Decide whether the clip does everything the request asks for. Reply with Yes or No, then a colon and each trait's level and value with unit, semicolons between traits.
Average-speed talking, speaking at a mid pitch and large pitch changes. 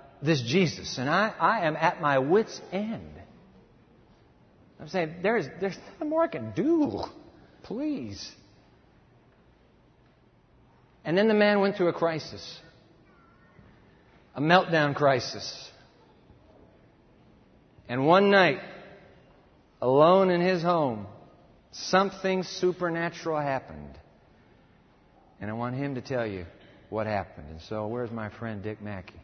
No: slow, 115 wpm; medium, 155 Hz; wide, 8.6 semitones